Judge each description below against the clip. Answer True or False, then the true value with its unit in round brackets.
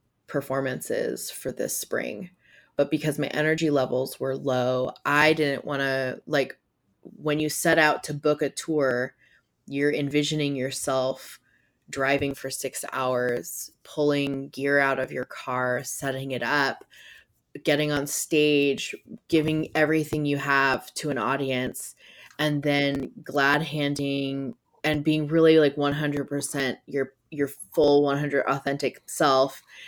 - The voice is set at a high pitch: False (140 Hz)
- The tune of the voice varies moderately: False (1.8 semitones)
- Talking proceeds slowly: True (130 wpm)